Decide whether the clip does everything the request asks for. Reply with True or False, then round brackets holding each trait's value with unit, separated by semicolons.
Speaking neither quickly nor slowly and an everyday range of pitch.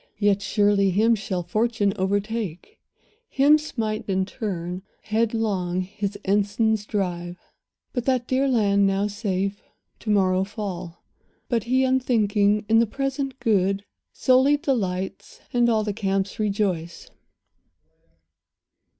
False (115 wpm; 3.1 semitones)